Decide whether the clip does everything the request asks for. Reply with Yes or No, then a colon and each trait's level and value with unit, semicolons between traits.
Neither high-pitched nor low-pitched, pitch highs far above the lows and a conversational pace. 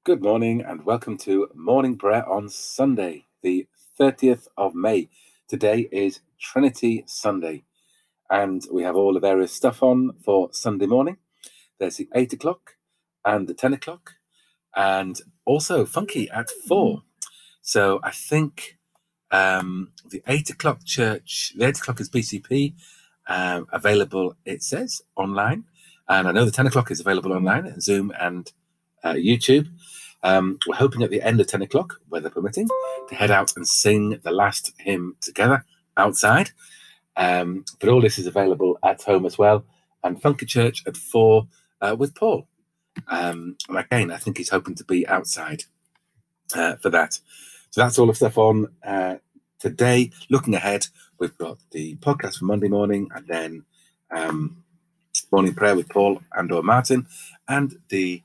No: low, 115 Hz; wide, 6.0 semitones; average, 155 wpm